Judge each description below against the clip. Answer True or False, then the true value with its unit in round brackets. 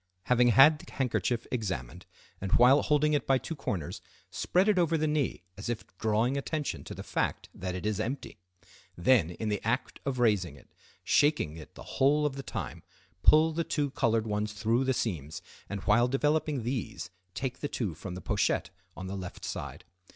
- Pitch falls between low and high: False (120 Hz)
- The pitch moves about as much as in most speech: False (5.8 semitones)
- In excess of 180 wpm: True (190 wpm)